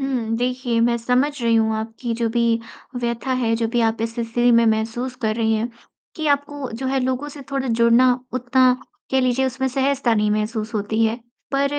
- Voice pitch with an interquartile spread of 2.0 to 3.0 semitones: Yes, narrow, 2.5 semitones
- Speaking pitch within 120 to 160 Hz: No, high, 240 Hz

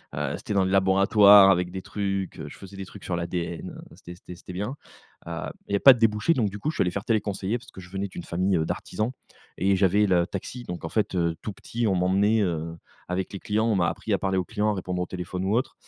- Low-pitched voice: Yes, very low, 95 Hz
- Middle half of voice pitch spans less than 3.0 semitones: Yes, narrow, 2.6 semitones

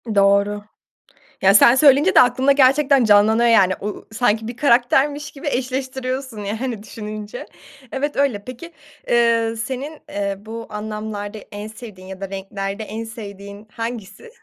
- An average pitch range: Yes, average, 4.1 semitones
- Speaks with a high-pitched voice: Yes, high, 225 Hz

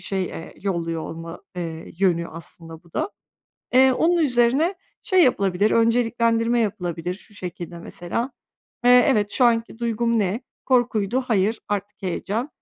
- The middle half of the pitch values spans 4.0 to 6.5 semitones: Yes, average, 5.3 semitones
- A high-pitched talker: Yes, high, 210 Hz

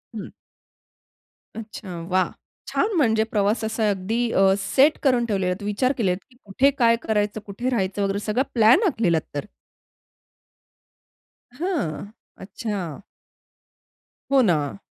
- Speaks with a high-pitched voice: Yes, high, 210 Hz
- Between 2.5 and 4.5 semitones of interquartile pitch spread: Yes, average, 3.7 semitones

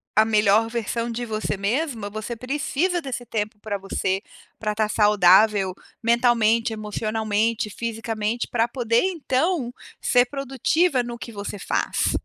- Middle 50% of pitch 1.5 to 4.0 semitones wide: Yes, narrow, 2.5 semitones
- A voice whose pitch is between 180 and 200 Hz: No, high, 225 Hz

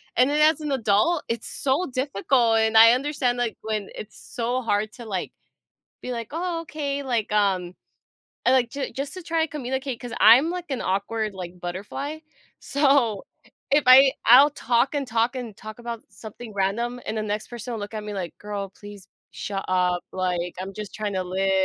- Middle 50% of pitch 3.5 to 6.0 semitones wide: Yes, average, 4.7 semitones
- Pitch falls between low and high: No, high, 230 Hz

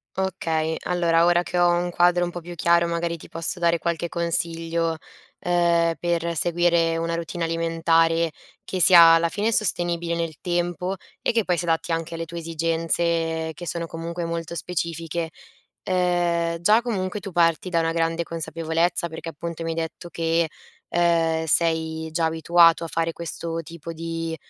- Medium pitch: Yes, medium, 170 Hz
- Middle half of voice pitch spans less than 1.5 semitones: Yes, narrow, 0.8 semitones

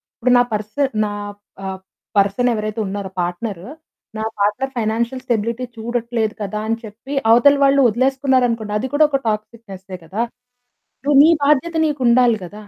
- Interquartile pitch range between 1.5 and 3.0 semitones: No, average, 3.5 semitones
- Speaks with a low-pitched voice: No, high, 230 Hz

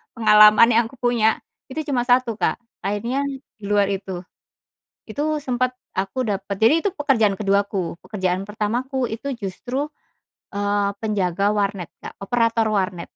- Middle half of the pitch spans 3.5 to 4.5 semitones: Yes, average, 4.0 semitones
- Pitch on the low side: No, high, 215 Hz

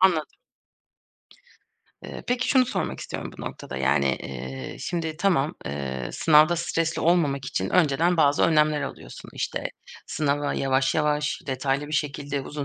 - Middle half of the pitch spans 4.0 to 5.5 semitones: No, average, 3.4 semitones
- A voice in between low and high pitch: Yes, medium, 150 Hz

